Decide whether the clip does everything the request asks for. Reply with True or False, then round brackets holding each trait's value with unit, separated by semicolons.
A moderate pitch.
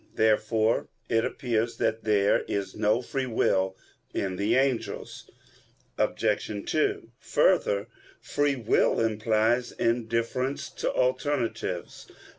False (115 Hz)